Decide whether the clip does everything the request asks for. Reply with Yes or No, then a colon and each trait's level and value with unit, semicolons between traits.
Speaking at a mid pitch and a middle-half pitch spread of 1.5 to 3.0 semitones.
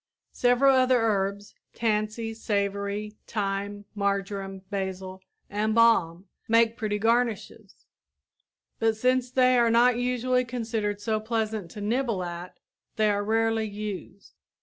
No: high, 215 Hz; narrow, 2.5 semitones